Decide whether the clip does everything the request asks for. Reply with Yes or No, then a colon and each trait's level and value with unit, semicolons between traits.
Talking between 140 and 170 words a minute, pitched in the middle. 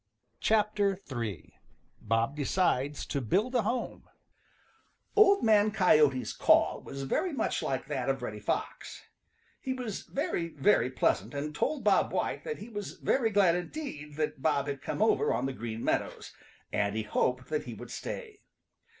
Yes: average, 160 wpm; medium, 150 Hz